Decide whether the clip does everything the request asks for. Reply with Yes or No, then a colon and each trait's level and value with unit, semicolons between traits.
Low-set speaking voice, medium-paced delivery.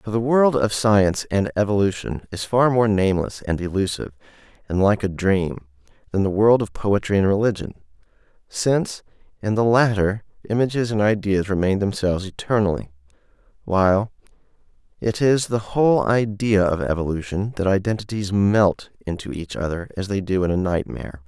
Yes: low, 100 Hz; average, 150 wpm